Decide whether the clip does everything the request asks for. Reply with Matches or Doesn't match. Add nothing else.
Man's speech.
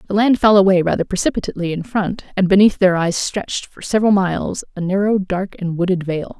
Doesn't match